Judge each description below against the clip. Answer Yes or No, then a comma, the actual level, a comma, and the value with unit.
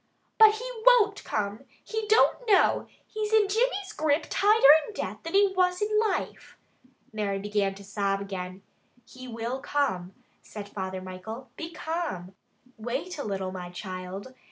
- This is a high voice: Yes, very high, 255 Hz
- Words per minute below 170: Yes, average, 155 wpm